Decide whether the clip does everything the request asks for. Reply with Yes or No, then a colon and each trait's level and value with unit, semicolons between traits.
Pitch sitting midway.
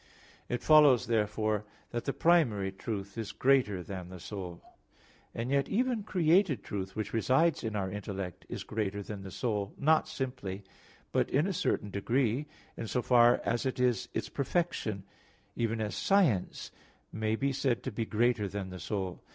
No: low, 115 Hz